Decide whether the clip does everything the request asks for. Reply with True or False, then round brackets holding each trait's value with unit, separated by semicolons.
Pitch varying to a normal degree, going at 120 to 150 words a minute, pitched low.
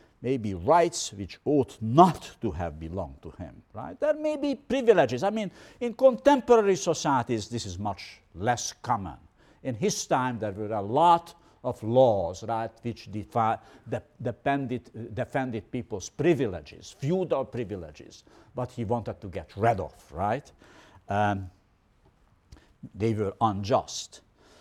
False (5.8 semitones; 140 wpm; 115 Hz)